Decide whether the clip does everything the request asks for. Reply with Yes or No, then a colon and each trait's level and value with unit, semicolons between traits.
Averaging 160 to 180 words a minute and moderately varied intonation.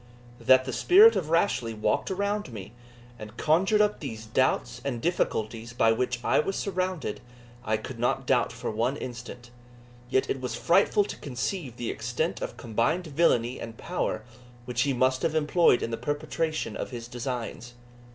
No: average, 170 wpm; wide, 5.9 semitones